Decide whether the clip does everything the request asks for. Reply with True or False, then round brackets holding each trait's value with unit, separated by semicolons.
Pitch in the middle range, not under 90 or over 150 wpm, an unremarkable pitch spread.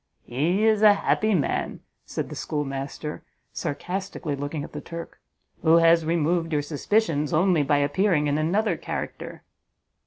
True (160 Hz; 145 wpm; 4.2 semitones)